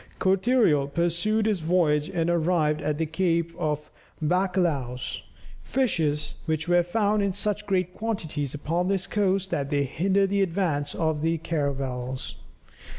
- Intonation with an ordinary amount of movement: Yes, average, 4.3 semitones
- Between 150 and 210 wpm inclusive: No, average, 140 wpm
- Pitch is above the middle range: No, medium, 170 Hz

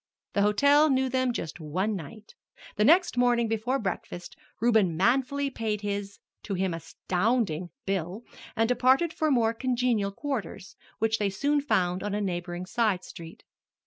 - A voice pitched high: Yes, high, 215 Hz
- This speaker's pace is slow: No, average, 150 wpm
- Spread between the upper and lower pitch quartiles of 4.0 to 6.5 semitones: Yes, average, 4.9 semitones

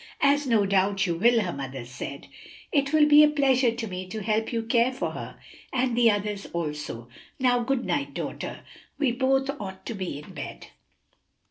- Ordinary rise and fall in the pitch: No, wide, 5.8 semitones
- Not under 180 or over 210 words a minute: Yes, average, 190 wpm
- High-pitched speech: Yes, high, 230 Hz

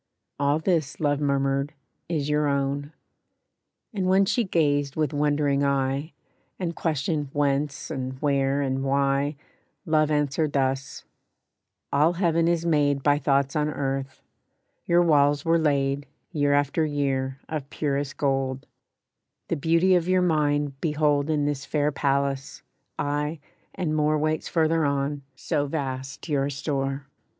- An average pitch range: No, narrow, 2.0 semitones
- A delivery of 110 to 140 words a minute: Yes, slow, 135 wpm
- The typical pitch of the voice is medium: Yes, medium, 145 Hz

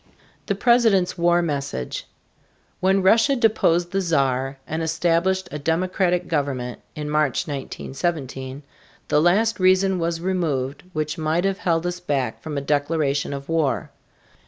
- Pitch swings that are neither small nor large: Yes, average, 4.5 semitones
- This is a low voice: No, medium, 165 Hz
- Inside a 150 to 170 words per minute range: No, slow, 135 wpm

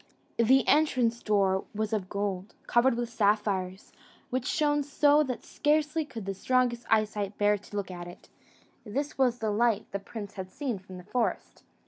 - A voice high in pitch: Yes, high, 220 Hz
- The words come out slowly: No, average, 170 wpm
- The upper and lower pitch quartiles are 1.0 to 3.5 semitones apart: No, average, 4.3 semitones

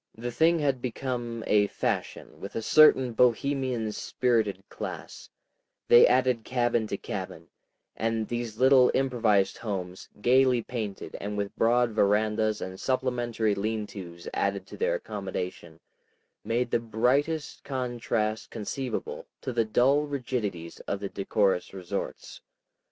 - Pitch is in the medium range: No, low, 115 Hz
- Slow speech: Yes, slow, 125 wpm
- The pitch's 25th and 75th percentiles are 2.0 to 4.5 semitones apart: Yes, average, 3.5 semitones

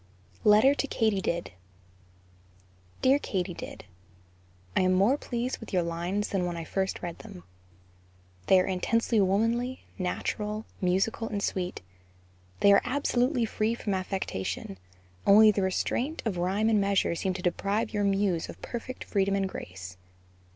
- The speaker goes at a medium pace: Yes, average, 145 wpm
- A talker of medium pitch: No, high, 200 Hz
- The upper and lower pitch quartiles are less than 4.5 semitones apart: Yes, average, 3.5 semitones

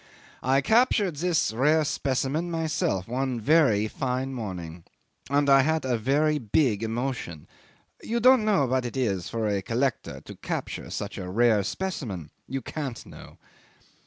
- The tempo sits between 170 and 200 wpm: No, average, 150 wpm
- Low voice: Yes, low, 130 Hz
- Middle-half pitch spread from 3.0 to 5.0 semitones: No, wide, 5.5 semitones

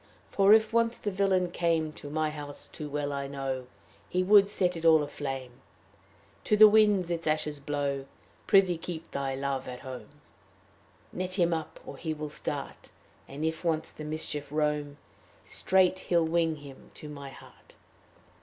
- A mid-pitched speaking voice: Yes, medium, 155 Hz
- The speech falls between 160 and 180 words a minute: Yes, average, 165 wpm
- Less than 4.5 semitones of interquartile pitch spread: Yes, average, 4.0 semitones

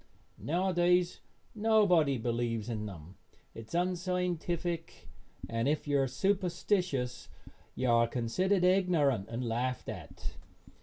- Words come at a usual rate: No, slow, 110 wpm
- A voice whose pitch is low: No, medium, 155 Hz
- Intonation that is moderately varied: No, wide, 7.3 semitones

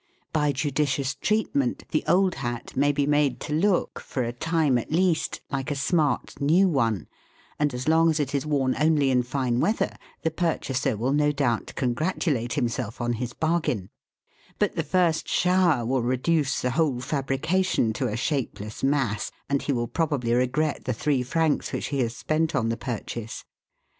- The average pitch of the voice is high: No, medium, 140 Hz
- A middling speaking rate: Yes, average, 175 wpm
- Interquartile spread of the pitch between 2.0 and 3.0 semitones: No, average, 4.2 semitones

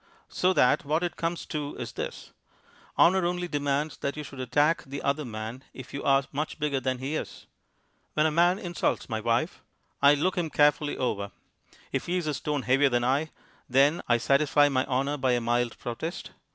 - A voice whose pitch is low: No, medium, 145 Hz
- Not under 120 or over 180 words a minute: No, average, 195 wpm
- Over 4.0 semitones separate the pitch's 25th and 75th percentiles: No, average, 3.3 semitones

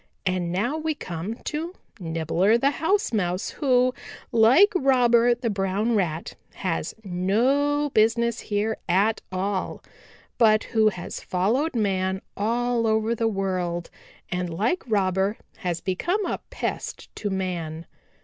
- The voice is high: Yes, high, 215 Hz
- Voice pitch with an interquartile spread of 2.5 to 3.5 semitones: No, average, 4.6 semitones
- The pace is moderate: No, slow, 130 wpm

